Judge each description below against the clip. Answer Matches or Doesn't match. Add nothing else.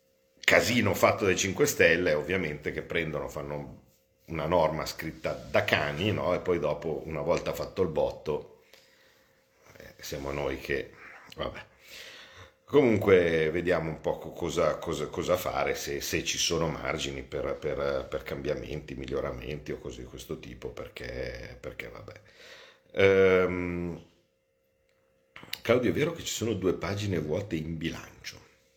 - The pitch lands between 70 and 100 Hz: Matches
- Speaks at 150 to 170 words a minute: Doesn't match